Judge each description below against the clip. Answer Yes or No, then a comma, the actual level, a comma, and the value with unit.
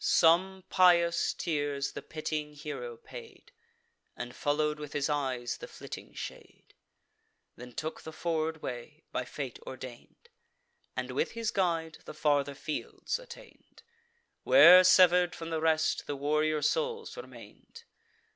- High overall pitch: No, medium, 155 Hz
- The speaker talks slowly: Yes, slow, 130 wpm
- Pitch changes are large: No, average, 3.9 semitones